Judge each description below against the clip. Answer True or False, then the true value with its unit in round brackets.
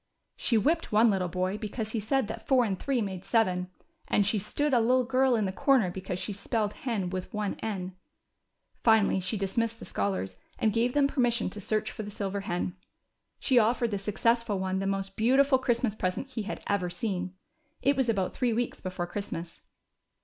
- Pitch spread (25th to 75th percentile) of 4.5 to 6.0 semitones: False (3.9 semitones)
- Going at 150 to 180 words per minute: False (195 wpm)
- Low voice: False (215 Hz)